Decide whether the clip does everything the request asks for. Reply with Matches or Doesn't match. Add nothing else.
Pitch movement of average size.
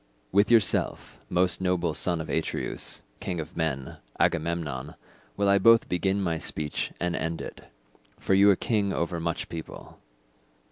Matches